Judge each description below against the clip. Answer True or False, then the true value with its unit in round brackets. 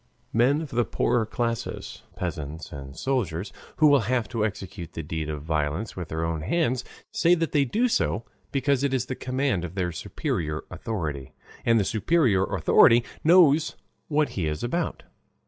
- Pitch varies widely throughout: True (9.0 semitones)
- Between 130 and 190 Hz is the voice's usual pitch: False (115 Hz)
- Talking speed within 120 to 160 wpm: False (170 wpm)